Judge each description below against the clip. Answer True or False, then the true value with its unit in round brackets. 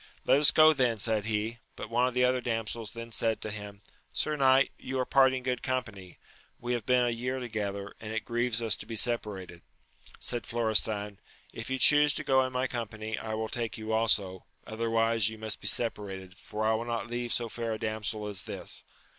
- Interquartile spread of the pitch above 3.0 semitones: False (2.4 semitones)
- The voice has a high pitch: False (115 Hz)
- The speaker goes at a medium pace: False (210 wpm)